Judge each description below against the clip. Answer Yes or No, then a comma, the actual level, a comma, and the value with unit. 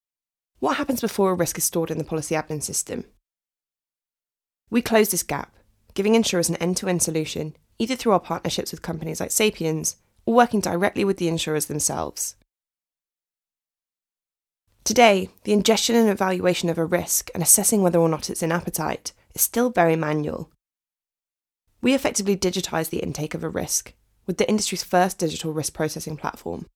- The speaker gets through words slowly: No, average, 165 wpm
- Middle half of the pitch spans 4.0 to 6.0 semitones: Yes, average, 4.4 semitones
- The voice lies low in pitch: No, medium, 175 Hz